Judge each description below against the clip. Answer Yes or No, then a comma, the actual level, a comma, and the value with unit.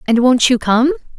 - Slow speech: No, fast, 205 wpm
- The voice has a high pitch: Yes, high, 240 Hz